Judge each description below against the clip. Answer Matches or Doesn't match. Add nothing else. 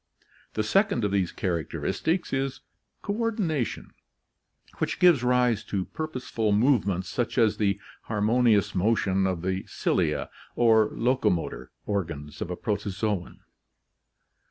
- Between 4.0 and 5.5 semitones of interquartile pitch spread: Matches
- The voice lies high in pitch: Doesn't match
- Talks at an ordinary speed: Doesn't match